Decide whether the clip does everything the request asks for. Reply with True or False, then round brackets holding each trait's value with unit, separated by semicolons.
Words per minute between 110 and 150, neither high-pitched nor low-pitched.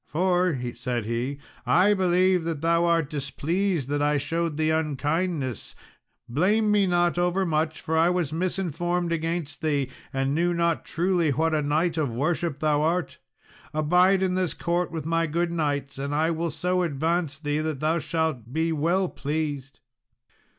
False (160 wpm; 160 Hz)